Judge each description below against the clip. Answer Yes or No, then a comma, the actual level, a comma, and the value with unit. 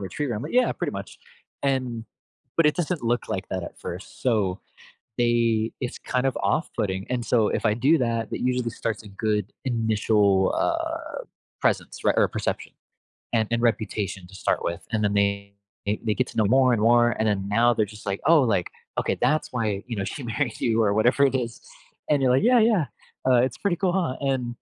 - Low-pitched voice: Yes, low, 115 Hz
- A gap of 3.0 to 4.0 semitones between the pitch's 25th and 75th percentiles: Yes, average, 3.6 semitones